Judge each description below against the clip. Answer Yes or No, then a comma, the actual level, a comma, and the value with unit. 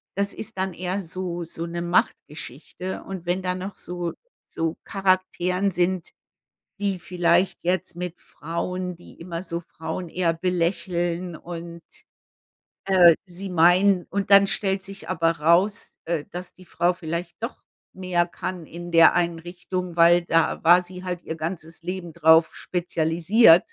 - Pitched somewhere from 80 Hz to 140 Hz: No, medium, 175 Hz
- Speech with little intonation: Yes, narrow, 1.7 semitones